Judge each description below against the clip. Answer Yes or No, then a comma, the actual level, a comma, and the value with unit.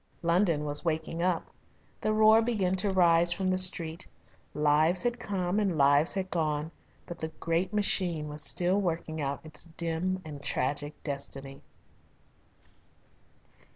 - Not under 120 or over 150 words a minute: Yes, average, 140 wpm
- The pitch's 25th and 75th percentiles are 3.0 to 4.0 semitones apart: Yes, average, 3.6 semitones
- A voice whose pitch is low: No, medium, 170 Hz